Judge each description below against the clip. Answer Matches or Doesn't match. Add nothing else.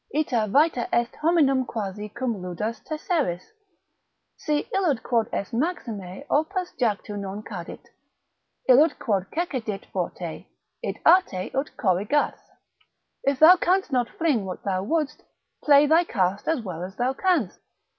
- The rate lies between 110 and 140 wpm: Matches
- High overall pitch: Matches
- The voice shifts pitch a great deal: Matches